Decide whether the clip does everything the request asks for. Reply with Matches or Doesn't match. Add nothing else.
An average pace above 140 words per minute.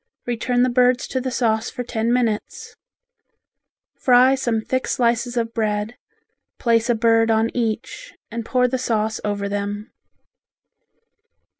Doesn't match